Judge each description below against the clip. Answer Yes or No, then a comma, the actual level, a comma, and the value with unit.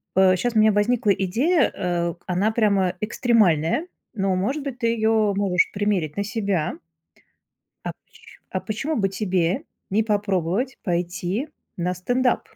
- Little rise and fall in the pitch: No, average, 4.1 semitones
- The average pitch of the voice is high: Yes, high, 205 Hz